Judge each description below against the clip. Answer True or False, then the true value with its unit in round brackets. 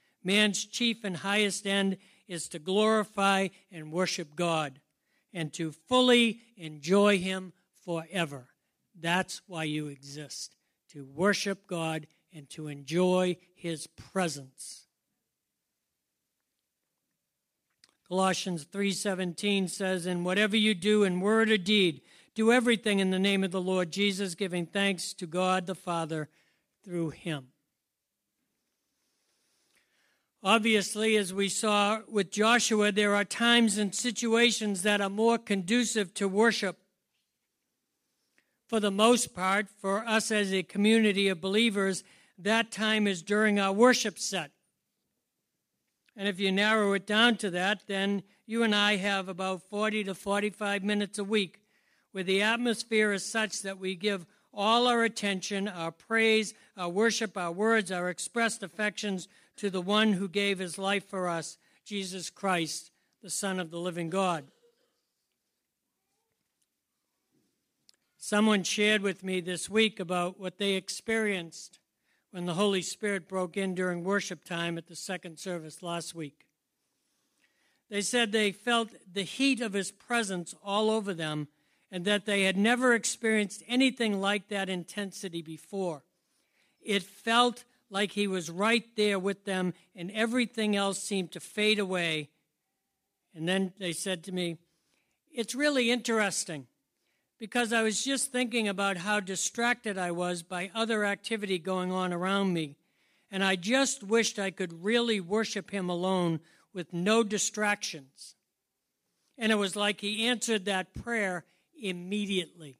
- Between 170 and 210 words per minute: False (140 wpm)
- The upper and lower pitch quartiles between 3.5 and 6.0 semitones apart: False (3.1 semitones)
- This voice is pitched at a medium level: False (200 Hz)